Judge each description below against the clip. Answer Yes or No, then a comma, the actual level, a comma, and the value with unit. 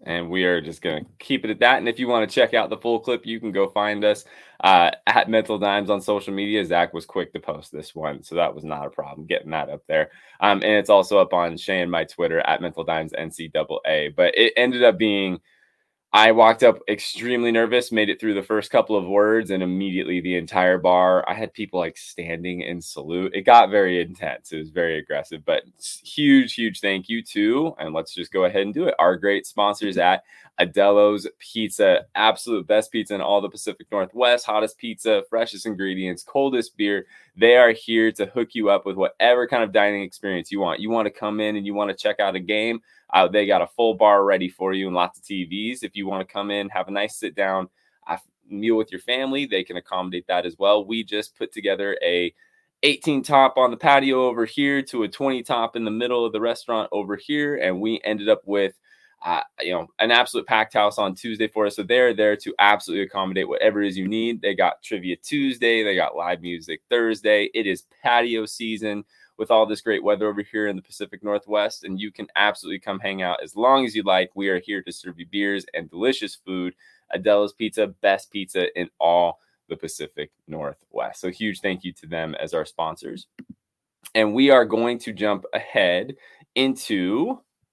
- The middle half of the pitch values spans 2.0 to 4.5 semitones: Yes, average, 3.4 semitones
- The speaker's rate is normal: No, fast, 220 wpm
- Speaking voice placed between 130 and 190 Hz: No, low, 105 Hz